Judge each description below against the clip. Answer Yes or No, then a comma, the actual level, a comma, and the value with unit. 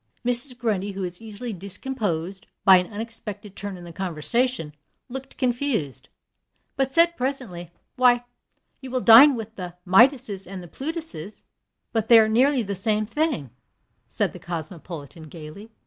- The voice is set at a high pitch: Yes, high, 215 Hz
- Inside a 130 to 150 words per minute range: Yes, average, 145 wpm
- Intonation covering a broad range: Yes, wide, 5.8 semitones